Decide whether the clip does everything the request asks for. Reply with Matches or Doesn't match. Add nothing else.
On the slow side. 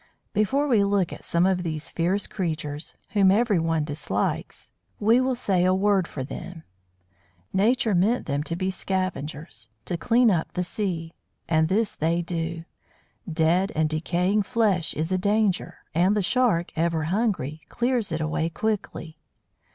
Doesn't match